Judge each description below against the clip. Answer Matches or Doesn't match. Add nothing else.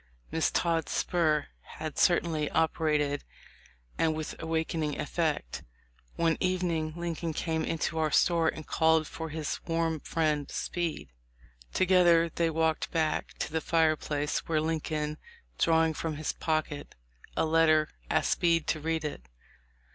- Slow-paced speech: Matches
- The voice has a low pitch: Doesn't match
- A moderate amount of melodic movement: Doesn't match